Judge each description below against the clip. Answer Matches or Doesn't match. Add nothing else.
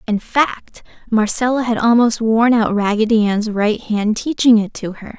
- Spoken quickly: Doesn't match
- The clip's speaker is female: Matches